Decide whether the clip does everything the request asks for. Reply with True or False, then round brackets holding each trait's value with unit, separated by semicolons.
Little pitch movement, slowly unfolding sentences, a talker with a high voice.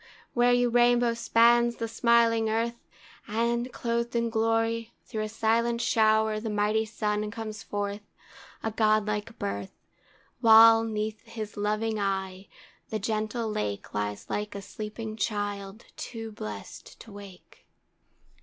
True (1.7 semitones; 130 wpm; 220 Hz)